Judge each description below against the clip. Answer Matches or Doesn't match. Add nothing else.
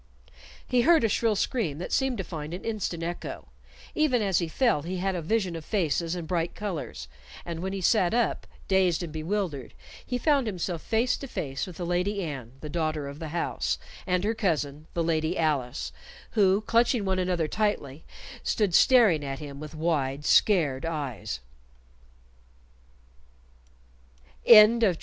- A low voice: Doesn't match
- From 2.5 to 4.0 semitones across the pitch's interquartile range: Doesn't match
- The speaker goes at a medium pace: Matches